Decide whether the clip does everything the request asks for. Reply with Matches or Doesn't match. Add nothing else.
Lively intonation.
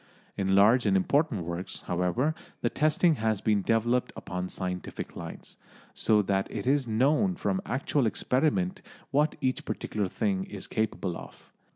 Matches